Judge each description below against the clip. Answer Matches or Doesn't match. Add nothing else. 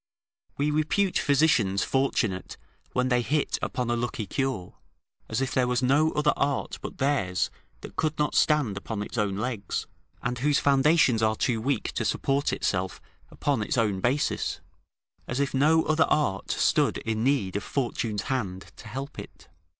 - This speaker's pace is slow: Doesn't match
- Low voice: Matches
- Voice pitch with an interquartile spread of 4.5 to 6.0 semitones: Matches